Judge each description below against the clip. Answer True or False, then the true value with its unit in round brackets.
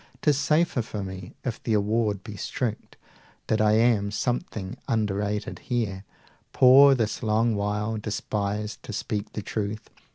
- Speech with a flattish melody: True (2.2 semitones)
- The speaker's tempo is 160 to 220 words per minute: False (140 wpm)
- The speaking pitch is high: False (110 Hz)